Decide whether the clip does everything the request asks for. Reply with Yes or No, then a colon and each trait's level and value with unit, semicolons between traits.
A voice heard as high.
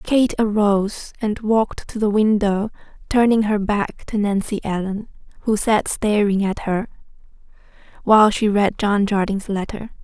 Yes: high, 210 Hz